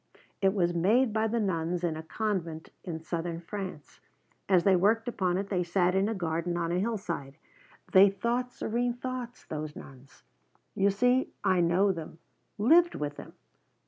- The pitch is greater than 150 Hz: Yes, high, 190 Hz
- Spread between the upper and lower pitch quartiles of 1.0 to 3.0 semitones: No, average, 4.5 semitones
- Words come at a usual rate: Yes, average, 170 wpm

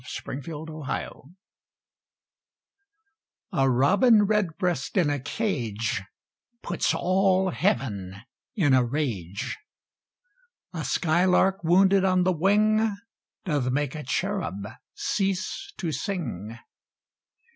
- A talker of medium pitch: Yes, medium, 165 Hz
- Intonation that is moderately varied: No, wide, 7.1 semitones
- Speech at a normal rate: No, slow, 100 wpm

